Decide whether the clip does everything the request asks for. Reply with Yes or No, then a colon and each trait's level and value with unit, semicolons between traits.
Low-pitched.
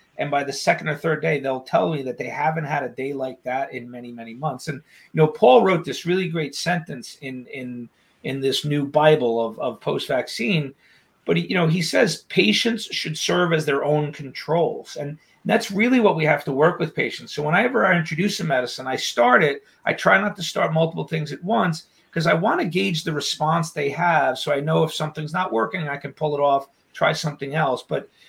No: medium, 155 Hz